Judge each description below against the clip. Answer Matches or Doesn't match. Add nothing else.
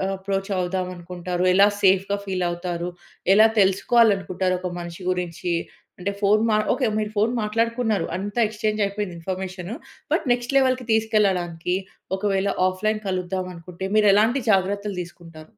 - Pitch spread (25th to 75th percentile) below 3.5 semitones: Matches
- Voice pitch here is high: Matches